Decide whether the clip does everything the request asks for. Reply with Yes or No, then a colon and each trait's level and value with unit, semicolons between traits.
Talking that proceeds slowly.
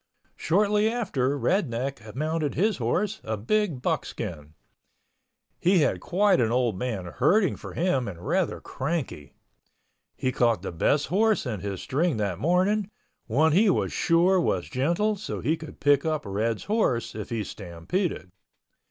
No: average, 150 wpm